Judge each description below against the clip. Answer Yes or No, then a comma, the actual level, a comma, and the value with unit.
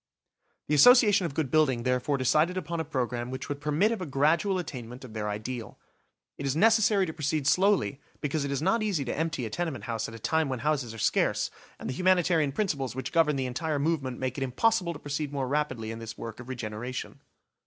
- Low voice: No, medium, 145 Hz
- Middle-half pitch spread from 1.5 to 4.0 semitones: No, average, 4.6 semitones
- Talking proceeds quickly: Yes, fast, 215 wpm